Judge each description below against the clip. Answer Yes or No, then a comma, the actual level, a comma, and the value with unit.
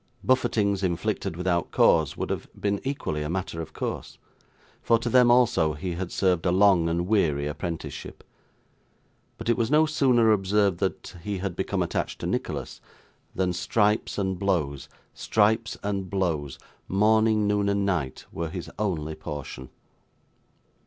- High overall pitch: No, very low, 95 Hz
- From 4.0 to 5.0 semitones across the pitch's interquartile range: Yes, average, 4.3 semitones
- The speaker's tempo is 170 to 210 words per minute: No, average, 150 wpm